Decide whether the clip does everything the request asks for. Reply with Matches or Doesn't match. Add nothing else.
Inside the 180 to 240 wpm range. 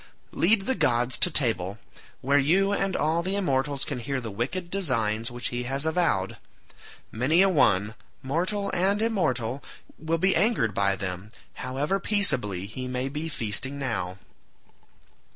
Doesn't match